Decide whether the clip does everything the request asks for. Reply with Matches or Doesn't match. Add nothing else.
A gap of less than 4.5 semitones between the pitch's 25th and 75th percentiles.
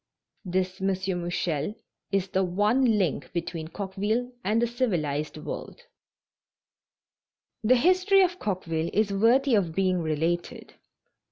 Doesn't match